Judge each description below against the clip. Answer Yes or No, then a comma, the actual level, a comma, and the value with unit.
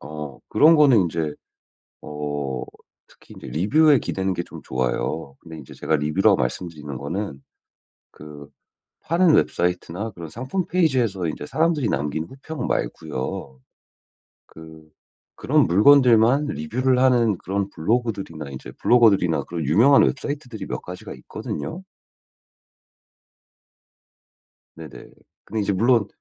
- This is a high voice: No, very low, 90 Hz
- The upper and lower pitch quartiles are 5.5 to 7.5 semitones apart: No, wide, 8.6 semitones